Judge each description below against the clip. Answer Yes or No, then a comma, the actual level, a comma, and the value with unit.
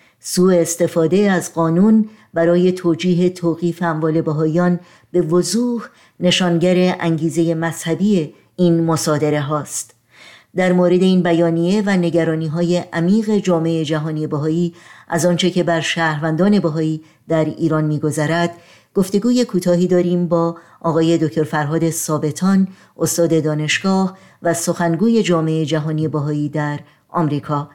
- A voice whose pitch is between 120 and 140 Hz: No, medium, 170 Hz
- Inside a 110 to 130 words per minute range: Yes, average, 115 wpm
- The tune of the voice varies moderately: No, narrow, 2.0 semitones